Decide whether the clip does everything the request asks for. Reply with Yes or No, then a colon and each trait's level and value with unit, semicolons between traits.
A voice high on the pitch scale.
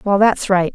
Yes: high, 195 Hz